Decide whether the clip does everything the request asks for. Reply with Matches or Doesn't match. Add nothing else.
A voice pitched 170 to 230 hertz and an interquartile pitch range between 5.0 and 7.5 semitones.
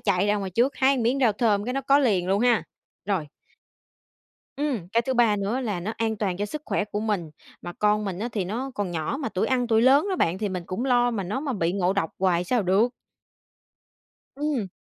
Doesn't match